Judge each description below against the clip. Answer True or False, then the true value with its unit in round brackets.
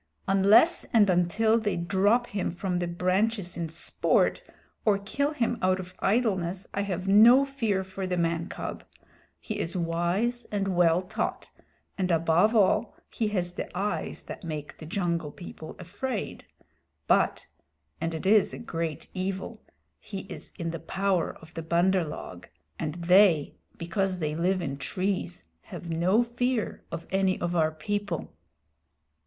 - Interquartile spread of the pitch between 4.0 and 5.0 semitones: False (3.3 semitones)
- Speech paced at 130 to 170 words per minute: True (155 wpm)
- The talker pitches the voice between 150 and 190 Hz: True (185 Hz)